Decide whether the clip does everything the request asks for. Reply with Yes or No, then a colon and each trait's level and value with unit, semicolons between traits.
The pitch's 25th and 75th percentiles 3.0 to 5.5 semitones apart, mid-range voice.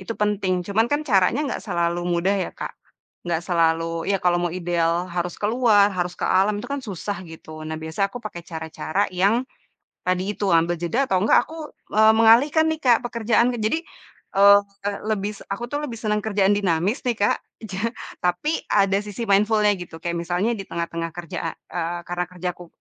No: average, 3.8 semitones; high, 195 Hz